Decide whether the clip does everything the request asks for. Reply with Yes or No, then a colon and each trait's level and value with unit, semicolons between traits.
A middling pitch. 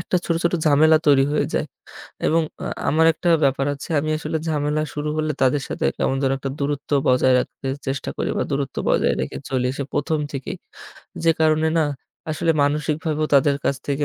Yes: medium, 145 Hz